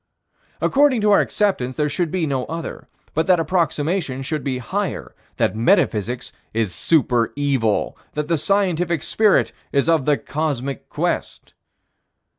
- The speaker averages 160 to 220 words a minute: No, average, 140 wpm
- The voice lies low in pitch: No, medium, 150 Hz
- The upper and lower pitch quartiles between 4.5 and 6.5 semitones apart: Yes, average, 5.2 semitones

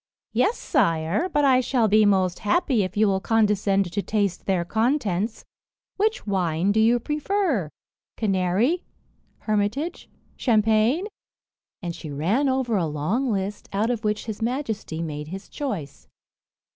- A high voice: Yes, high, 210 Hz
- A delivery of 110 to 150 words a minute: Yes, average, 140 wpm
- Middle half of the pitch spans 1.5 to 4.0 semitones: No, average, 4.7 semitones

